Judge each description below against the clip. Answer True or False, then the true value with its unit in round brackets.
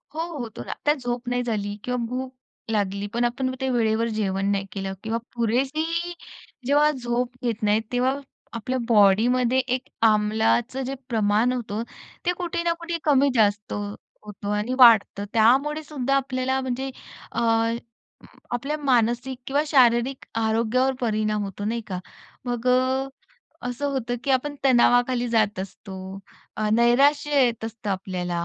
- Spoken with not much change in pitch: False (3.4 semitones)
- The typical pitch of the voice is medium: False (245 Hz)